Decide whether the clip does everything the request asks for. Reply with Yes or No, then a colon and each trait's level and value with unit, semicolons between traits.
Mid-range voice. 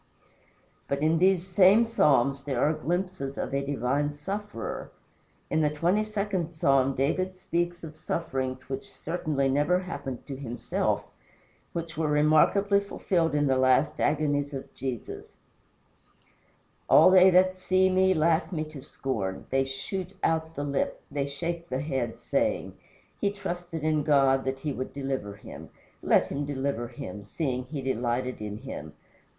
Yes: medium, 145 Hz